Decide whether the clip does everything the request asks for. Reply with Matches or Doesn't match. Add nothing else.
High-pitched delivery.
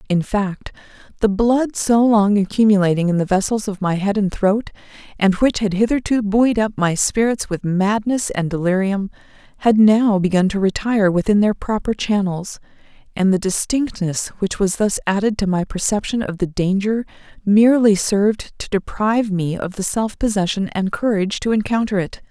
Matches